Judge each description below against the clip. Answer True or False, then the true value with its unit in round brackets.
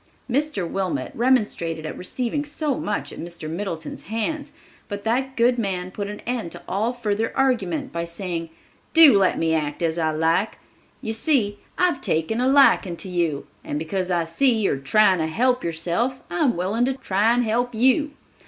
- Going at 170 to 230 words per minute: True (180 wpm)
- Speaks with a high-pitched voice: True (205 Hz)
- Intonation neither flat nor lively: False (6.6 semitones)